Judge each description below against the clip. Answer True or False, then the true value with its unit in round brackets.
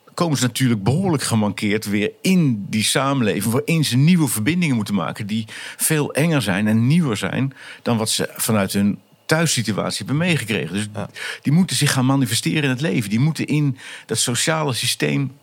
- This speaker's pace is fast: False (175 wpm)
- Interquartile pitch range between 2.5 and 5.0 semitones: False (5.6 semitones)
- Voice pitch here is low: True (130 Hz)